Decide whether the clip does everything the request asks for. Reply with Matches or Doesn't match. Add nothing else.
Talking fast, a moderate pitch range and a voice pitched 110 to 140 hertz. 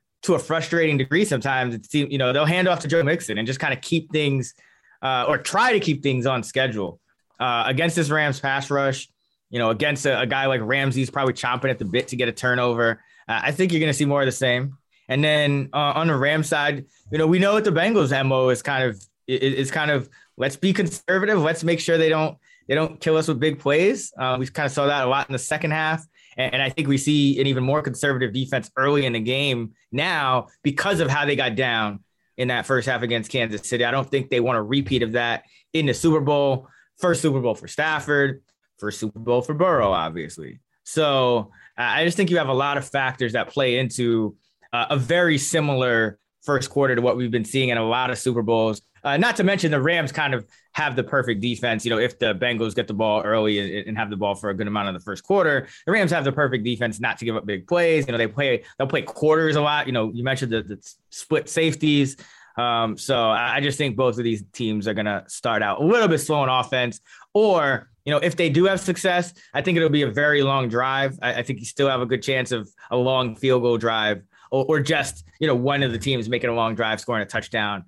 Matches